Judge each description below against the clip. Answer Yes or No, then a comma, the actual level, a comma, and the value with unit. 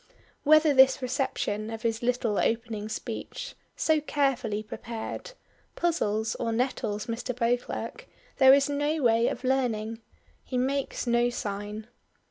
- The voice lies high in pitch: Yes, high, 240 Hz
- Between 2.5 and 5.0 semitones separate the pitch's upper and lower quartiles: Yes, average, 3.3 semitones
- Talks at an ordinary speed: No, slow, 125 wpm